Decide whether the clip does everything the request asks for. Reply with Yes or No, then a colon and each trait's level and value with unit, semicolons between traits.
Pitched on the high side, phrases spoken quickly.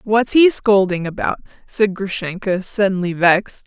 No: high, 200 Hz; slow, 130 wpm